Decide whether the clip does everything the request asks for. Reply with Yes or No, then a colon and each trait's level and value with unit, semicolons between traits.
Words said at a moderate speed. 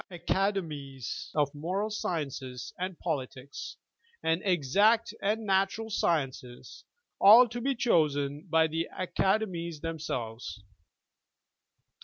No: slow, 105 wpm